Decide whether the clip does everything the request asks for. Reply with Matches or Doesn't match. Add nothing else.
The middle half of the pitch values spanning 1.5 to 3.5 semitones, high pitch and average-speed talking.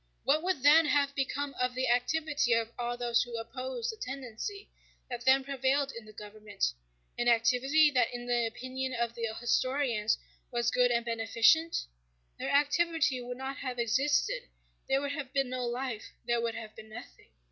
Matches